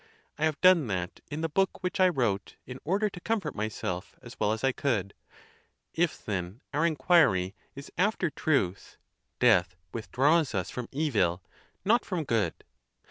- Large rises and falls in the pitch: Yes, wide, 8.7 semitones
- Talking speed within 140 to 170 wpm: Yes, average, 160 wpm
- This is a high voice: No, low, 135 Hz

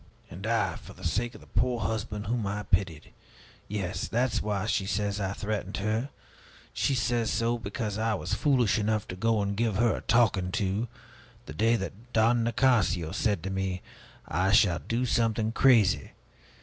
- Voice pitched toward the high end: No, low, 105 Hz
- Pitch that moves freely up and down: No, average, 3.0 semitones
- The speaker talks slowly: No, average, 185 wpm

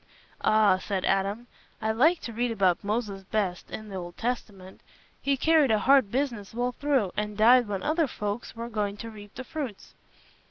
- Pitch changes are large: No, average, 3.7 semitones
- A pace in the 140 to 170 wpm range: No, average, 185 wpm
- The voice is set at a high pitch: Yes, high, 220 Hz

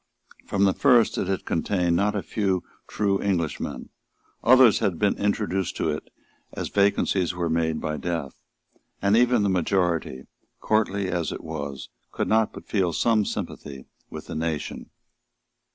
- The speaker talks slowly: No, average, 150 wpm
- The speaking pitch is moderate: No, very low, 95 Hz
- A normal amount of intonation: Yes, average, 3.9 semitones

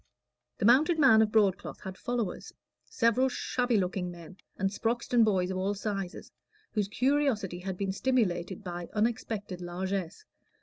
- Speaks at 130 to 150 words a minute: Yes, average, 140 wpm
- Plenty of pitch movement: No, average, 4.1 semitones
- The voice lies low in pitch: No, high, 200 Hz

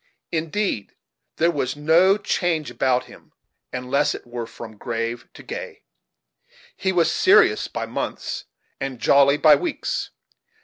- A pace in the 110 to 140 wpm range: Yes, slow, 135 wpm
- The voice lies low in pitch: No, medium, 145 Hz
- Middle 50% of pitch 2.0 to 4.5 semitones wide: No, wide, 5.5 semitones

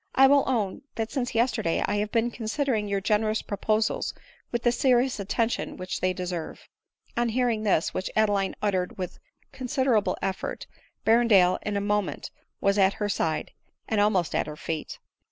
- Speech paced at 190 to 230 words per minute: No, average, 170 wpm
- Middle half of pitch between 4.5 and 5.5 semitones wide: No, average, 3.5 semitones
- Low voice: No, high, 210 Hz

